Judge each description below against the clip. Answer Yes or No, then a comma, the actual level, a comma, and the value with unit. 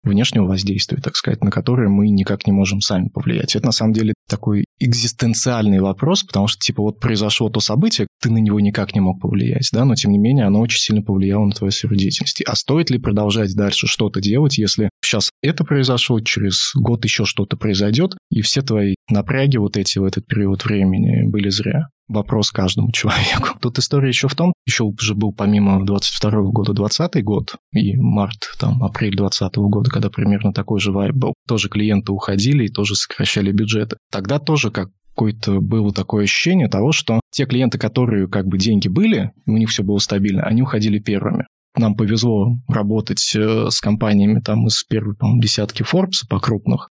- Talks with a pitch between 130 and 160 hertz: No, low, 105 Hz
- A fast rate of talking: Yes, fast, 185 wpm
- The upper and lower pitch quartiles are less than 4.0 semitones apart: Yes, average, 3.2 semitones